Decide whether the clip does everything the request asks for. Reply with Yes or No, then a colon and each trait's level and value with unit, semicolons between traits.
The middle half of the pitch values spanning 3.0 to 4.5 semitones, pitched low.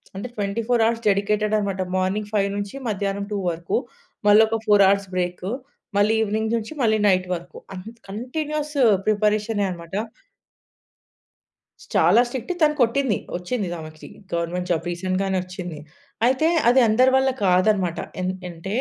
No: average, 3.4 semitones; high, 205 Hz